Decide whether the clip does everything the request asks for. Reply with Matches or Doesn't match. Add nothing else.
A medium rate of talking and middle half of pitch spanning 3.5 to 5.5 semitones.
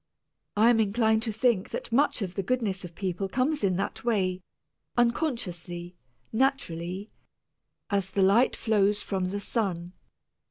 Matches